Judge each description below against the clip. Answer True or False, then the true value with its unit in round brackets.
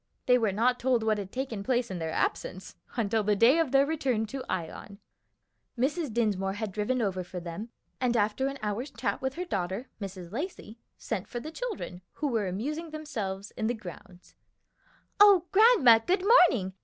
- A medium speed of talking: True (180 wpm)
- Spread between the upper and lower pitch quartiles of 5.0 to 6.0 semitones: True (5.5 semitones)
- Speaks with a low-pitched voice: False (230 Hz)